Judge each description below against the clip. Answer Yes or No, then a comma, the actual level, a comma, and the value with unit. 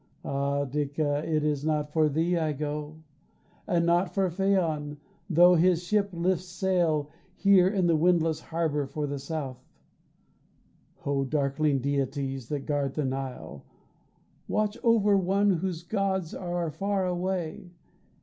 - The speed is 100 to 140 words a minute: Yes, slow, 135 wpm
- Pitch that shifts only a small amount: No, average, 3.9 semitones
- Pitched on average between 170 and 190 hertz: No, medium, 160 Hz